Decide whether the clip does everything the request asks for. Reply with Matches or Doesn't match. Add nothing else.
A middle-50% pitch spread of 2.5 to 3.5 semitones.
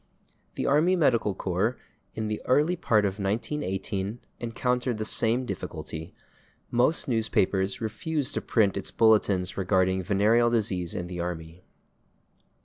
Doesn't match